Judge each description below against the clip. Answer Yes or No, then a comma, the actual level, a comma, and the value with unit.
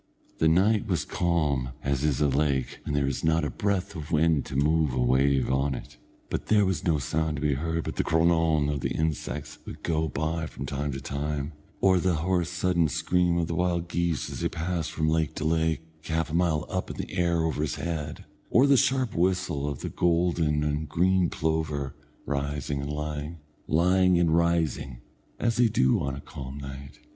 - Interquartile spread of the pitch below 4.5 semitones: Yes, average, 3.1 semitones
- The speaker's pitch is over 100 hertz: No, very low, 80 Hz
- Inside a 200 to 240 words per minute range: Yes, fast, 205 wpm